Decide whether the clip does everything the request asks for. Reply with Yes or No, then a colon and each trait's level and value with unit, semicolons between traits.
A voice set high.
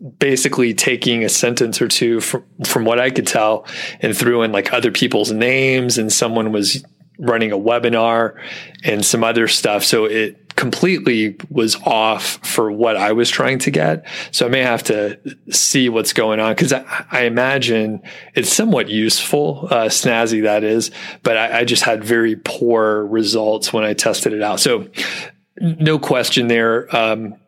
No: low, 115 Hz